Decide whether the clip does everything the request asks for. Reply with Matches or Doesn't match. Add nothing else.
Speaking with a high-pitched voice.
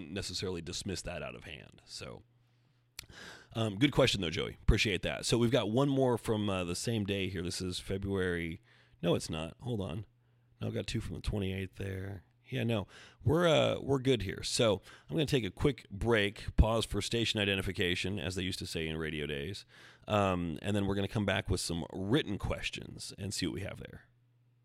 Doesn't match